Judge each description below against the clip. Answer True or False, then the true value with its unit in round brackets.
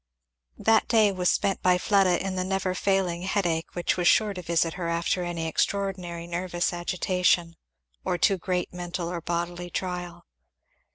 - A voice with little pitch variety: True (1.6 semitones)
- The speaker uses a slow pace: False (160 wpm)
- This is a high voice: False (180 Hz)